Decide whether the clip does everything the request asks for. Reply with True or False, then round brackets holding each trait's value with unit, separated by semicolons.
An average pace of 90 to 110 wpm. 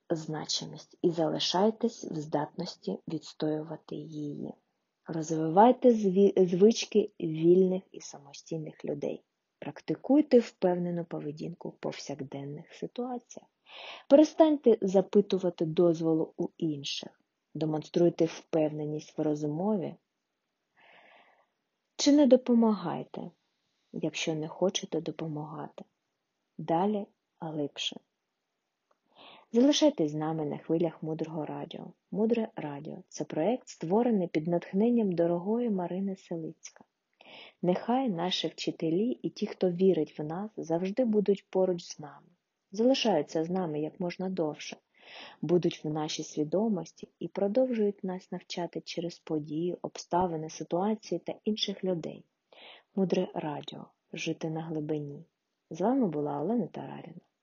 True (105 wpm)